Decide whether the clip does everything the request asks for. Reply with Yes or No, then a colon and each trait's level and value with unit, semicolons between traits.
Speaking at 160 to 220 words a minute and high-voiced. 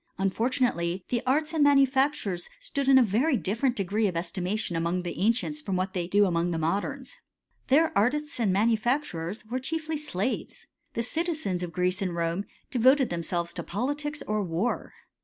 Yes: average, 175 wpm; high, 215 Hz